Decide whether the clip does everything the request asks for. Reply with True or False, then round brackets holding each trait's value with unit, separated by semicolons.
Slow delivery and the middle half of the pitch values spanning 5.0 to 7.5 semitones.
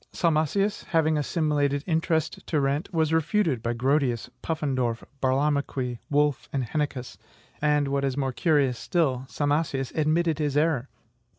False (130 wpm; 3.0 semitones)